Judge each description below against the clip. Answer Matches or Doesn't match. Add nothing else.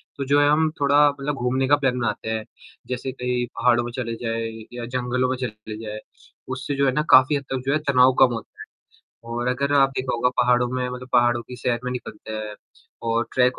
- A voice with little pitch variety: Matches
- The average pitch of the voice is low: Matches